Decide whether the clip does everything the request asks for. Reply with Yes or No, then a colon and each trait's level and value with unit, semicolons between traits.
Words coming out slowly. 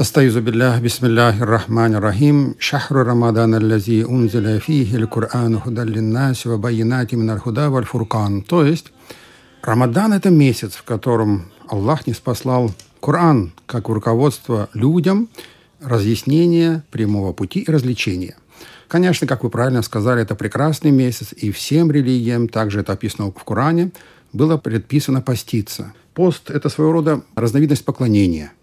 Yes: slow, 95 wpm